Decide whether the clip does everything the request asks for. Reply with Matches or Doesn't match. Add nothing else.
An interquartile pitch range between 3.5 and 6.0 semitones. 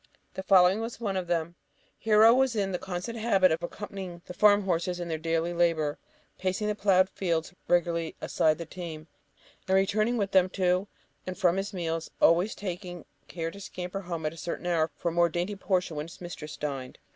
Doesn't match